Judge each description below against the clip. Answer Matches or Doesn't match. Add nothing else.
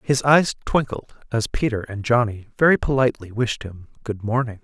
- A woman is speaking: Doesn't match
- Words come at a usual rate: Matches